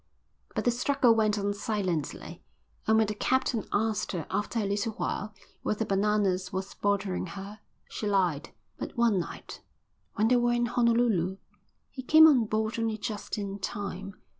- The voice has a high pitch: Yes, high, 210 Hz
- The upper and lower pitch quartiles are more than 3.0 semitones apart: No, average, 2.7 semitones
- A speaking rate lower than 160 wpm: No, average, 165 wpm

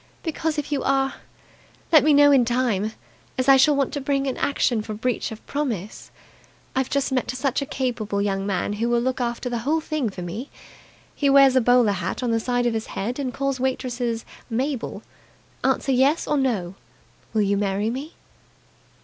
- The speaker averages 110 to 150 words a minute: No, average, 190 wpm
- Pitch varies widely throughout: No, average, 3.6 semitones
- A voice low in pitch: No, very high, 250 Hz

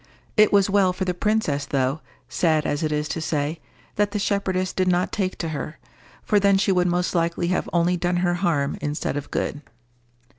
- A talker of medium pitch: Yes, medium, 175 Hz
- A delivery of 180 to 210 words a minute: Yes, average, 200 wpm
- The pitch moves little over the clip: No, average, 3.7 semitones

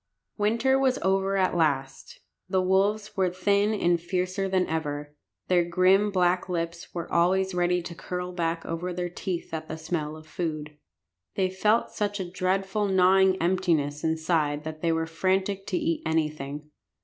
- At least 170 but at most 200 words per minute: No, average, 160 wpm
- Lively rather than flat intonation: No, average, 2.9 semitones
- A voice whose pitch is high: No, medium, 180 Hz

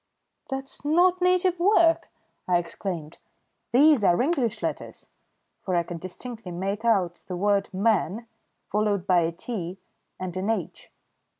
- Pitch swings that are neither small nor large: No, wide, 6.9 semitones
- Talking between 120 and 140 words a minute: Yes, slow, 135 wpm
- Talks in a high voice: Yes, high, 205 Hz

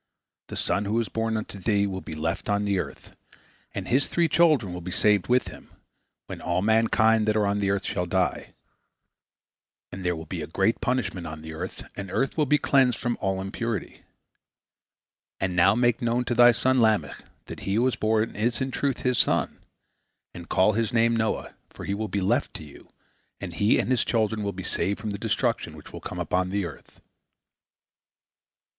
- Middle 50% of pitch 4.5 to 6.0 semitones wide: No, average, 3.6 semitones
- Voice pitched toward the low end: Yes, low, 105 Hz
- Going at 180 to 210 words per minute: Yes, fast, 205 wpm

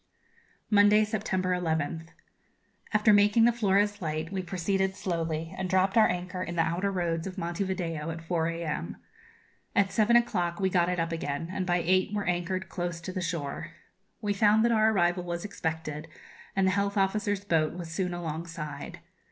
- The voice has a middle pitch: Yes, medium, 180 Hz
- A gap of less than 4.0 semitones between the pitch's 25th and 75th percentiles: Yes, average, 3.2 semitones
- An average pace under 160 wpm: No, average, 175 wpm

